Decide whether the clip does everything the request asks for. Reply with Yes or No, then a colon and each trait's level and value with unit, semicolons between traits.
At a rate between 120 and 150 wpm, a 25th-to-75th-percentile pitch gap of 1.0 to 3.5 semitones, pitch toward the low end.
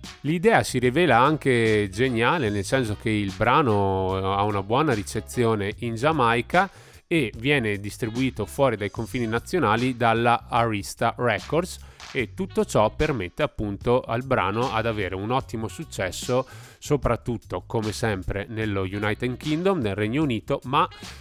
No: average, 135 wpm; average, 3.9 semitones; low, 115 Hz